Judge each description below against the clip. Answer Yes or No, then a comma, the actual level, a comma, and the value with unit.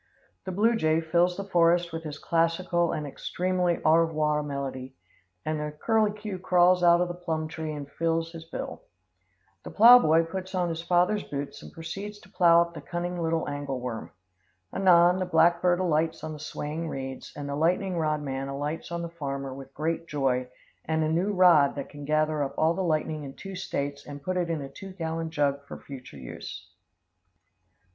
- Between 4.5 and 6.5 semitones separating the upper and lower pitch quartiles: No, average, 3.2 semitones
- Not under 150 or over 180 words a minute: No, average, 195 wpm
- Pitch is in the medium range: Yes, medium, 165 Hz